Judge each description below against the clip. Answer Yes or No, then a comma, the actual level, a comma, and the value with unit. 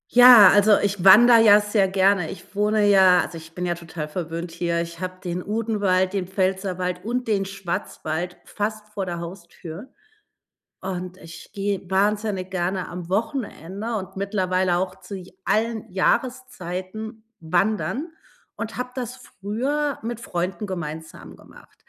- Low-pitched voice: No, high, 190 Hz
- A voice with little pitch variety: No, average, 3.1 semitones